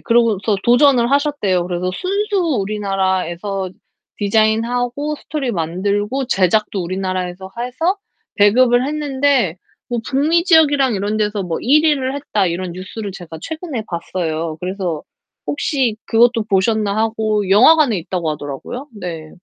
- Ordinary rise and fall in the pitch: No, wide, 6.1 semitones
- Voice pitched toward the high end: Yes, high, 215 Hz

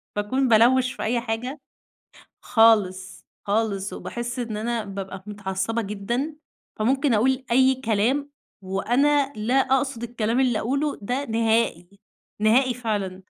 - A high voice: Yes, high, 230 Hz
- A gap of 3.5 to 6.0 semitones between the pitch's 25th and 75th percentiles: Yes, average, 3.8 semitones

